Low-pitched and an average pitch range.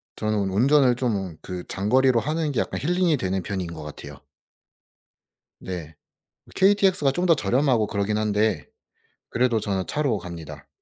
No: low, 110 Hz; wide, 6.5 semitones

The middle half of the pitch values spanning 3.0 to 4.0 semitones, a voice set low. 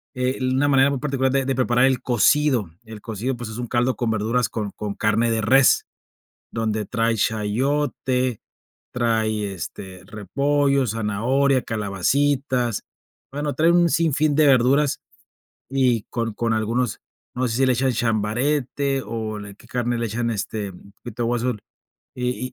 Yes: average, 3.4 semitones; low, 120 Hz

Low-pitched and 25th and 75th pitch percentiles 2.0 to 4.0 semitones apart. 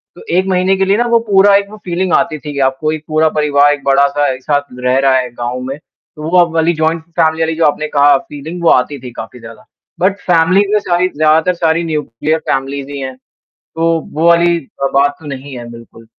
No: medium, 155 Hz; average, 3.7 semitones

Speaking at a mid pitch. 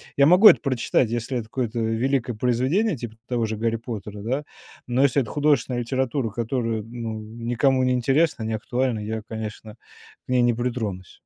No: low, 120 Hz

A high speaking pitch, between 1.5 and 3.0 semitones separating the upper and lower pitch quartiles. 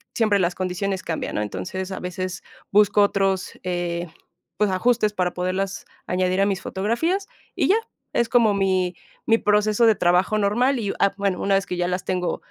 Yes: high, 195 Hz; narrow, 2.4 semitones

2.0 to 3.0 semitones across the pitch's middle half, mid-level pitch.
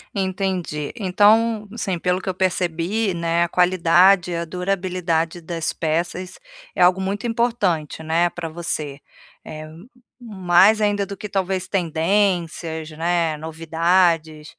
Yes: average, 2.7 semitones; medium, 180 Hz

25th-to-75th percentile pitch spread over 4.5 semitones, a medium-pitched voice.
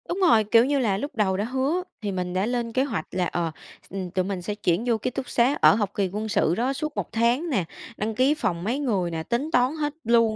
No: average, 5.3 semitones; high, 225 Hz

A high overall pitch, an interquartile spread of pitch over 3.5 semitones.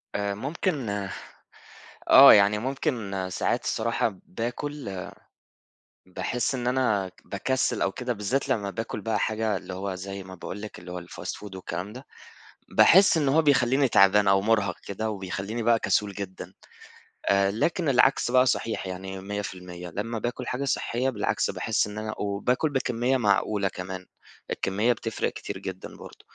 No: low, 105 Hz; average, 4.1 semitones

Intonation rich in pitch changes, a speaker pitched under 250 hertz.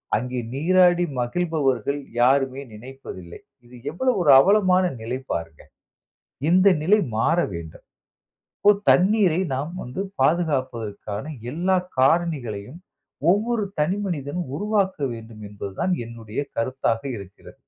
Yes: wide, 7.7 semitones; medium, 140 Hz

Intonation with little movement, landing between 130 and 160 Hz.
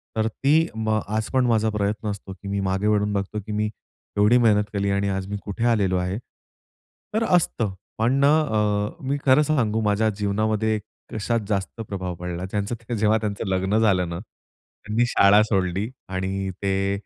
No: narrow, 2.1 semitones; low, 105 Hz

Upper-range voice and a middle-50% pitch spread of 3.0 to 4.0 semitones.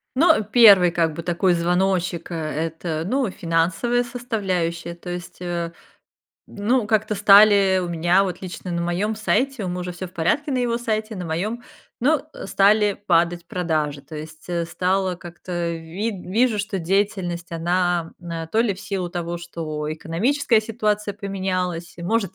No: medium, 180 Hz; average, 3.6 semitones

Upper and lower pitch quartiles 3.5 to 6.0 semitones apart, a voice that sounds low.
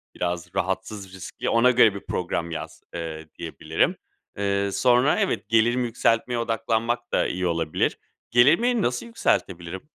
Yes: average, 5.3 semitones; low, 105 Hz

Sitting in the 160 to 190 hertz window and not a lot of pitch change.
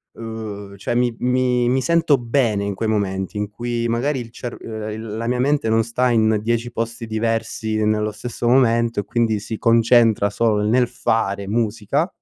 No: low, 115 Hz; narrow, 2.0 semitones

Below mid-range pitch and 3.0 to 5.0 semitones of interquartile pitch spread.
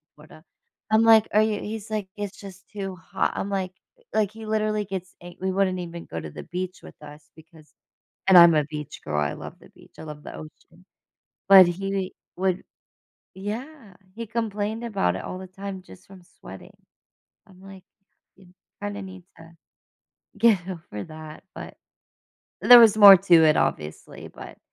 No: high, 190 Hz; average, 3.5 semitones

